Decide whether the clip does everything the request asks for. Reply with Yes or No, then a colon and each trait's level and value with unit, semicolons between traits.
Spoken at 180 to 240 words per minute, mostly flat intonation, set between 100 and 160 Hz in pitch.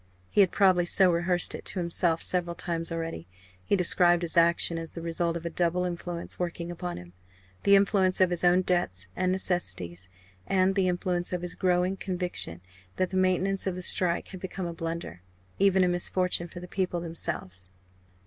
No: average, 185 wpm; narrow, 1.6 semitones; medium, 175 Hz